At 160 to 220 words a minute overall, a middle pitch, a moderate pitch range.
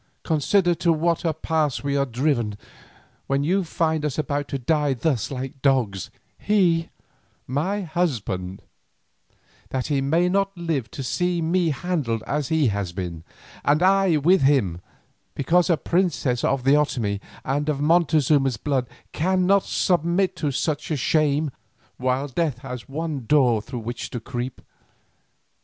No: average, 145 wpm; medium, 145 Hz; average, 4.7 semitones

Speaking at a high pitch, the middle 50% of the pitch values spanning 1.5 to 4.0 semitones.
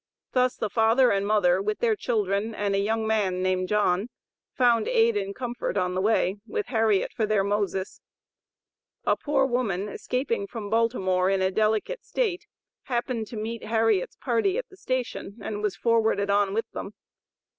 Yes: high, 215 Hz; average, 3.3 semitones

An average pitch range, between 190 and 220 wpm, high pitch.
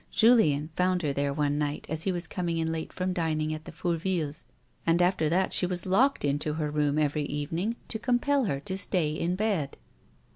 No: average, 3.6 semitones; fast, 205 wpm; medium, 165 Hz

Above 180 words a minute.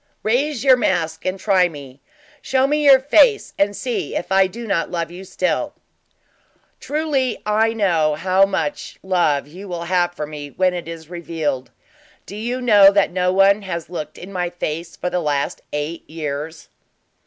No: average, 175 wpm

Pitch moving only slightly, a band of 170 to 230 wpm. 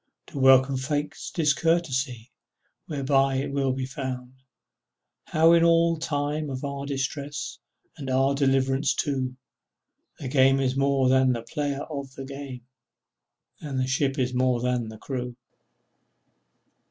No: narrow, 1.7 semitones; average, 140 wpm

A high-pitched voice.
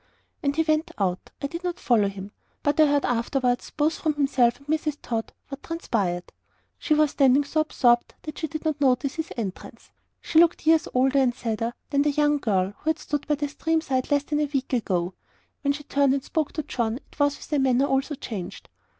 Yes: very high, 280 Hz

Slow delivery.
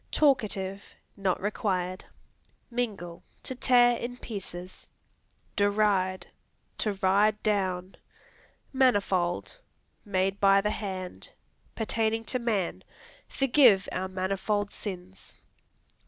Yes: slow, 90 wpm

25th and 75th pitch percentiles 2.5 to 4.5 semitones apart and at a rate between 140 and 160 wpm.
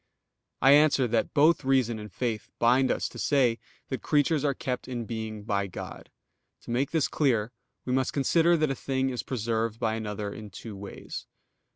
No: average, 3.7 semitones; average, 185 wpm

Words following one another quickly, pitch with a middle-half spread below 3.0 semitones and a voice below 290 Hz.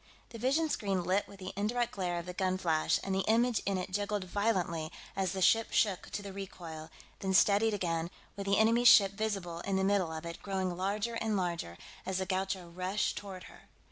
Yes: fast, 210 wpm; narrow, 2.4 semitones; high, 190 Hz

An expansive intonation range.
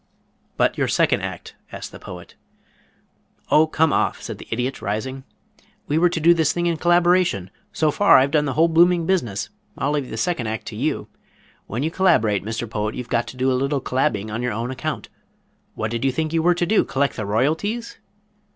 Yes: wide, 6.0 semitones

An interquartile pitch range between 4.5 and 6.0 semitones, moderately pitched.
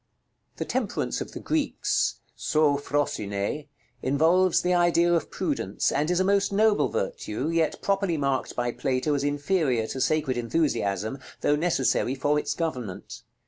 Yes: average, 5.0 semitones; medium, 145 Hz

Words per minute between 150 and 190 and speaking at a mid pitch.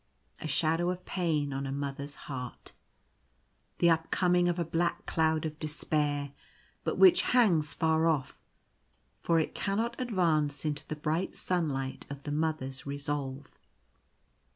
No: average, 140 wpm; medium, 155 Hz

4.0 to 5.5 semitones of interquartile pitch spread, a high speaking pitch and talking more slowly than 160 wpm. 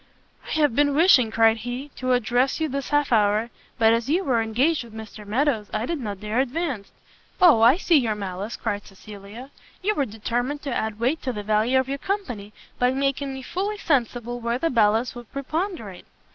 No: average, 4.3 semitones; high, 245 Hz; average, 200 wpm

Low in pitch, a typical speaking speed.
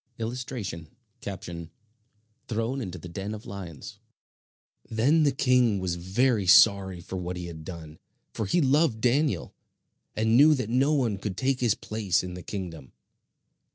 Yes: low, 110 Hz; average, 150 wpm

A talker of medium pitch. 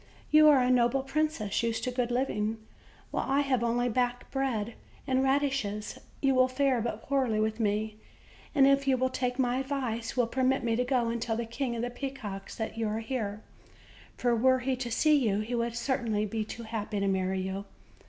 No: high, 240 Hz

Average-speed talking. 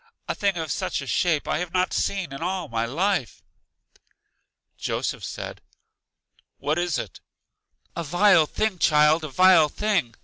Yes: average, 150 wpm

